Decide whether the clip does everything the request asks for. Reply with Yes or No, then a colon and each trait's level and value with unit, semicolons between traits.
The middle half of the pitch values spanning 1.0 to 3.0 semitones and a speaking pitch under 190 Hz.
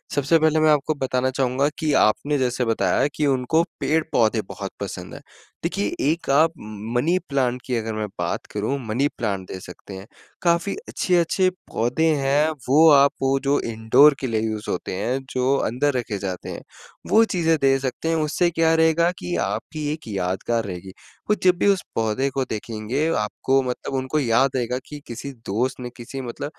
No: average, 5.3 semitones; low, 135 Hz